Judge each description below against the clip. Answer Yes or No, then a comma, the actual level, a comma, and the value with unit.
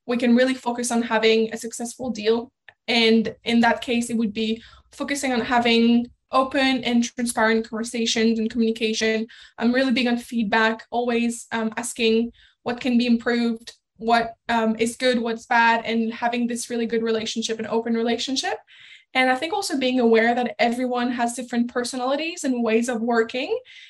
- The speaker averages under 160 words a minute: No, average, 170 wpm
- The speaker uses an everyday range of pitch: No, narrow, 1.4 semitones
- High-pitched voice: Yes, high, 235 Hz